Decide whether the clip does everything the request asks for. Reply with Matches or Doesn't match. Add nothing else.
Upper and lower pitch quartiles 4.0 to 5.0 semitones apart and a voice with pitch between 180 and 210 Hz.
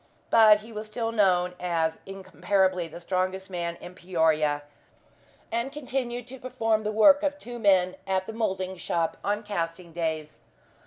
Matches